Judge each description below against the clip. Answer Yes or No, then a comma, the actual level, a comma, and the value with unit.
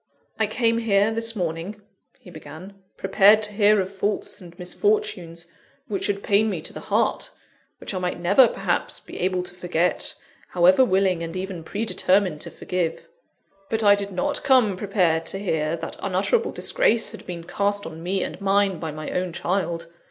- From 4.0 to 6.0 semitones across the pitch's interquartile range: No, average, 3.0 semitones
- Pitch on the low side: No, high, 190 Hz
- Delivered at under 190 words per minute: Yes, average, 175 wpm